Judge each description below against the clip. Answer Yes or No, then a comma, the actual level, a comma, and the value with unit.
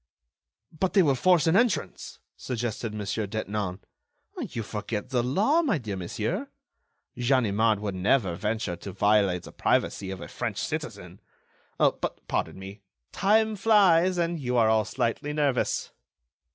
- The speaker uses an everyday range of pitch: No, wide, 8.1 semitones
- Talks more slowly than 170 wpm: Yes, average, 140 wpm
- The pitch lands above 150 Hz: No, low, 115 Hz